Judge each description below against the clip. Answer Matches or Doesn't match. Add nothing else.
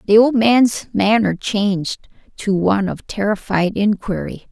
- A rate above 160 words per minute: Doesn't match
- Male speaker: Doesn't match